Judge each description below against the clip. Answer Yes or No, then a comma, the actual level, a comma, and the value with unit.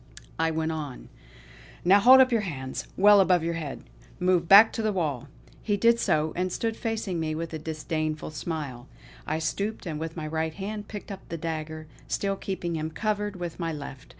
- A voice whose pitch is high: No, medium, 165 Hz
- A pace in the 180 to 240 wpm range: Yes, average, 195 wpm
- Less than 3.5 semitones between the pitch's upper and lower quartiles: No, average, 4.4 semitones